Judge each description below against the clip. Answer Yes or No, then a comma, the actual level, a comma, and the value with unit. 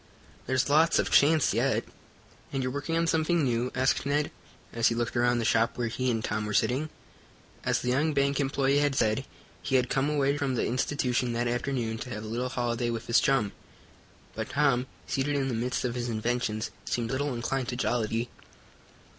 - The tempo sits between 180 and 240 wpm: Yes, average, 195 wpm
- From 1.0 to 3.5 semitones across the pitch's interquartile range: Yes, average, 2.9 semitones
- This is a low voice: Yes, low, 125 Hz